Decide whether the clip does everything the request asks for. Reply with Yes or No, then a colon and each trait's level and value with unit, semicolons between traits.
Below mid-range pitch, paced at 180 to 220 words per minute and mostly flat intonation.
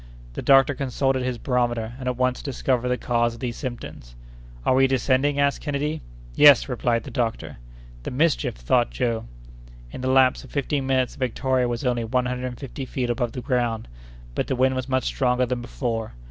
Yes: low, 125 Hz; average, 195 wpm; narrow, 1.8 semitones